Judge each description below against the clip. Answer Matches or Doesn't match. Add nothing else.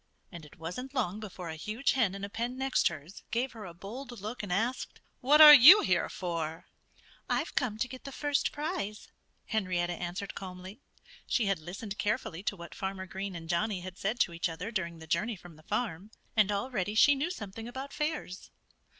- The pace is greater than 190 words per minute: Matches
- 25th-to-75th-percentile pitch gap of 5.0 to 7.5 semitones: Matches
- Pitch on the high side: Matches